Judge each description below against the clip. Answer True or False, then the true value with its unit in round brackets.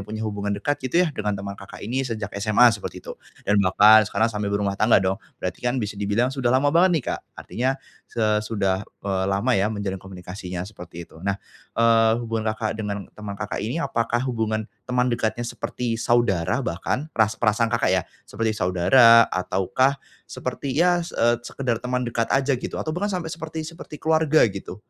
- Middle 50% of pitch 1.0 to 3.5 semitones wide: False (3.9 semitones)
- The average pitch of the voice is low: True (110 Hz)